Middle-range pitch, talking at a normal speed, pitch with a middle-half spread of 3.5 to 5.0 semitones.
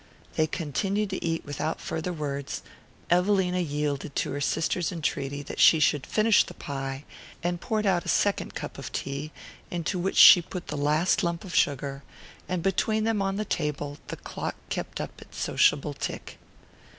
Yes: medium, 165 Hz; average, 175 wpm; average, 4.5 semitones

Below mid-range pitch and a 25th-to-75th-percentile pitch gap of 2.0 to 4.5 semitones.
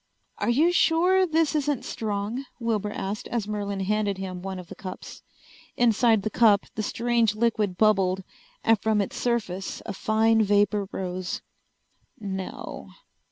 No: high, 210 Hz; average, 3.2 semitones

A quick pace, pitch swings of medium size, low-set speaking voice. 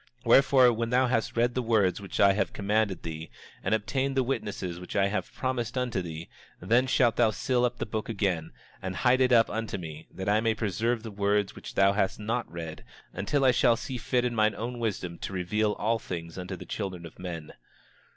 Yes: fast, 220 wpm; average, 4.2 semitones; low, 110 Hz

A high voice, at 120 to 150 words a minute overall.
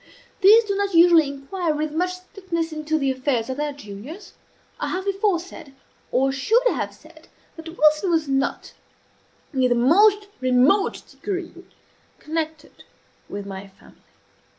Yes: very high, 315 Hz; average, 145 wpm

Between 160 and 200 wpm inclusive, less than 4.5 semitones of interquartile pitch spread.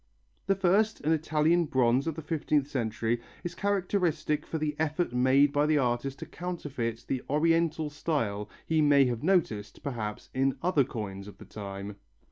No: average, 165 wpm; average, 5.2 semitones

